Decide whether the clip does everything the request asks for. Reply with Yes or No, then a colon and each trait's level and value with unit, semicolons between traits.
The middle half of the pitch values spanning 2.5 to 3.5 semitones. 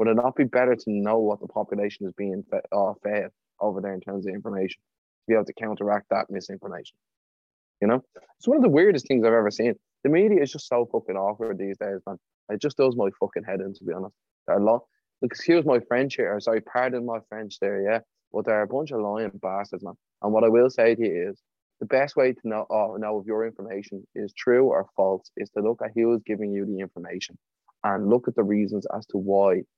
Yes: average, 2.8 semitones